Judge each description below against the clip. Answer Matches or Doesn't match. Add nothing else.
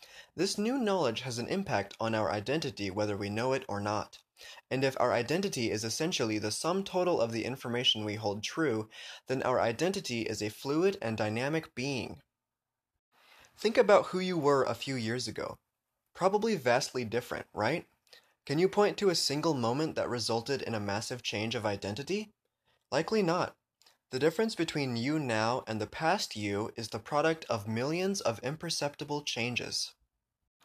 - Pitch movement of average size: Doesn't match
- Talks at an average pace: Matches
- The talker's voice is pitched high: Doesn't match